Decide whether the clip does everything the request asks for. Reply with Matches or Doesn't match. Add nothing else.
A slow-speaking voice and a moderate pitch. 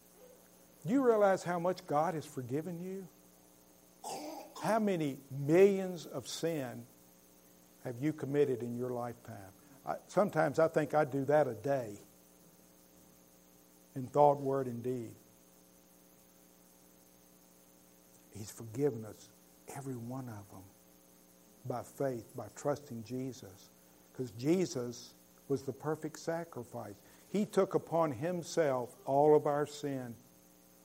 Doesn't match